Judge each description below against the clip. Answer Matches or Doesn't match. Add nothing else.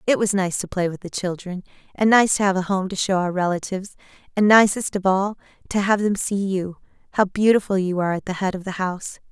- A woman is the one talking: Matches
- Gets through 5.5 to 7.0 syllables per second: Matches